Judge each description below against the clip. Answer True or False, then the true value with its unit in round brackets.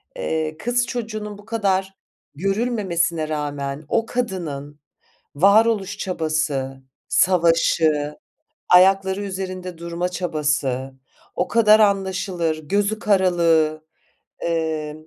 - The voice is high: False (180 Hz)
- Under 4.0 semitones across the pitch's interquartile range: False (4.4 semitones)